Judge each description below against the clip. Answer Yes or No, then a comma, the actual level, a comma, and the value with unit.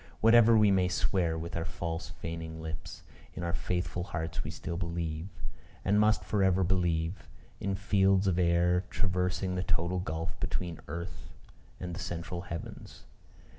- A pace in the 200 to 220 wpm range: No, average, 155 wpm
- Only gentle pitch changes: Yes, narrow, 2.1 semitones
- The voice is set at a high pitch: No, very low, 90 Hz